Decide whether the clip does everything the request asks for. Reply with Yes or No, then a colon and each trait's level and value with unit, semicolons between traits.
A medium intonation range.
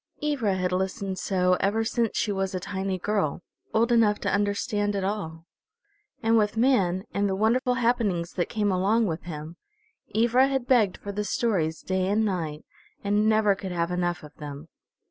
Yes: average, 3.3 semitones